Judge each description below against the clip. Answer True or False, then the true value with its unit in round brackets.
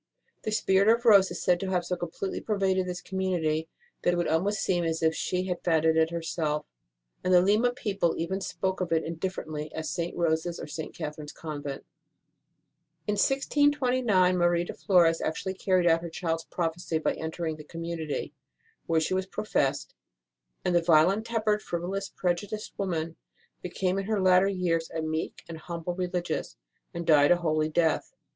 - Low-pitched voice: False (175 Hz)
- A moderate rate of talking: True (180 wpm)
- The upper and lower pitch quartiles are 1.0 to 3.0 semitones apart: True (2.7 semitones)